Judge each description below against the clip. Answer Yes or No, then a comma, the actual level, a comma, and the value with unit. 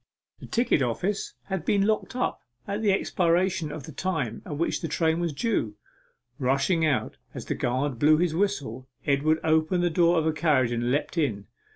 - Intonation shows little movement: No, average, 4.6 semitones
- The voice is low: No, medium, 160 Hz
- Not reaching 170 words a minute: No, average, 190 wpm